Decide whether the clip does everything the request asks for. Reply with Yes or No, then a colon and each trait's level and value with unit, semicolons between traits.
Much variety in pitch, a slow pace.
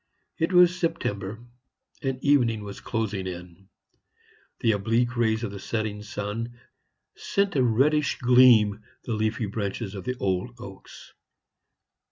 No: average, 3.6 semitones; slow, 130 wpm